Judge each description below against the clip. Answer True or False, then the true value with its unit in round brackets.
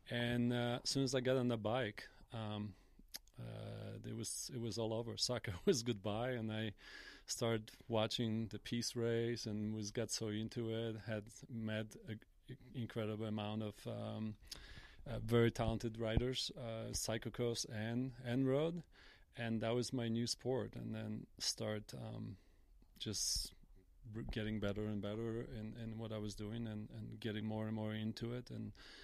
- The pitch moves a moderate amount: False (1.8 semitones)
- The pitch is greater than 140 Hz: False (110 Hz)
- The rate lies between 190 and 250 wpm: False (170 wpm)